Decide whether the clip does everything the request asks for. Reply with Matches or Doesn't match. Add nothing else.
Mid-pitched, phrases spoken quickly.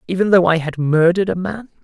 Matches